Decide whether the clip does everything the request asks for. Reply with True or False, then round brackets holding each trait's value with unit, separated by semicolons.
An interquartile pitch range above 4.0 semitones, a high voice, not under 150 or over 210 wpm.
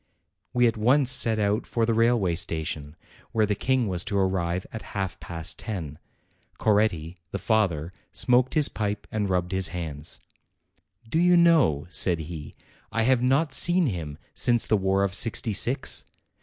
False (5.6 semitones; 105 Hz; 170 wpm)